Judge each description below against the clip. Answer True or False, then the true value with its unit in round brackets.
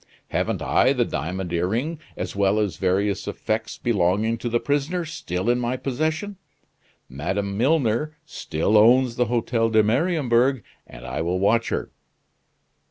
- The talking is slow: False (145 wpm)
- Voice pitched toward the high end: False (115 Hz)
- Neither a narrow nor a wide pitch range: True (5.0 semitones)